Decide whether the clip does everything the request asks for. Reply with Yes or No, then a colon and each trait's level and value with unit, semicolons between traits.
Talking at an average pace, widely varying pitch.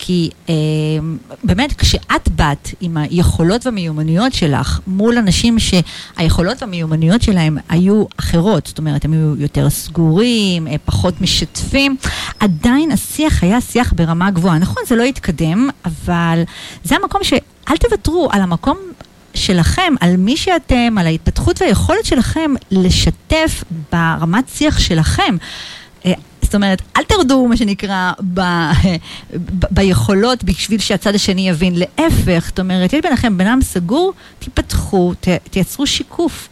Yes: average, 125 wpm; wide, 6.4 semitones